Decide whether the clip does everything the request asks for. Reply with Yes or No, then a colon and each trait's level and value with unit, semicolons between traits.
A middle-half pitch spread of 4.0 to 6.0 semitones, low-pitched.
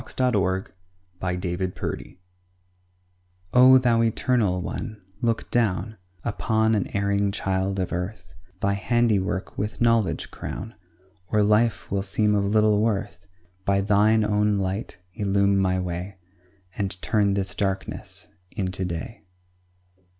No: average, 2.7 semitones; low, 100 Hz